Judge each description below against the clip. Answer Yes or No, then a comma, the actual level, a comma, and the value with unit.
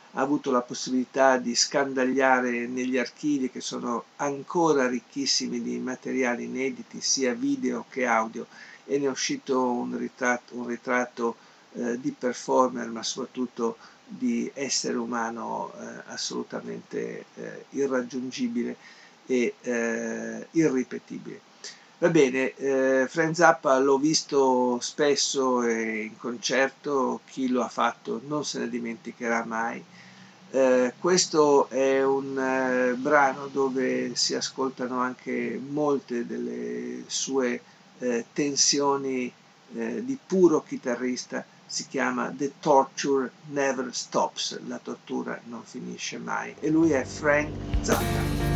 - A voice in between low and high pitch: No, low, 130 Hz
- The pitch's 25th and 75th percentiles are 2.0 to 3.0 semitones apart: Yes, narrow, 2.5 semitones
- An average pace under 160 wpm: Yes, average, 120 wpm